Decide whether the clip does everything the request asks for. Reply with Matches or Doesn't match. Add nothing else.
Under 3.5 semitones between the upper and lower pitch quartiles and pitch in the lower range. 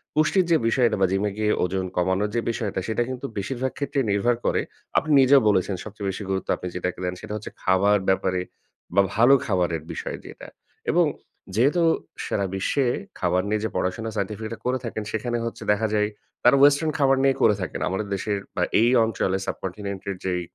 Doesn't match